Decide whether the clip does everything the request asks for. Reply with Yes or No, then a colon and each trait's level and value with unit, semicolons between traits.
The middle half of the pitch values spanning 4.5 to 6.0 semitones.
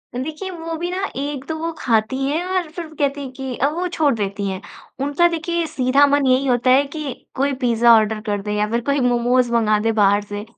Yes: average, 5.3 semitones